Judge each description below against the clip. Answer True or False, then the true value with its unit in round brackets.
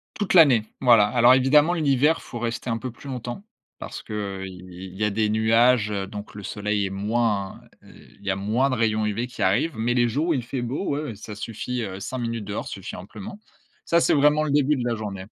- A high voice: False (115 Hz)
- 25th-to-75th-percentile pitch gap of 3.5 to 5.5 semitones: True (4.1 semitones)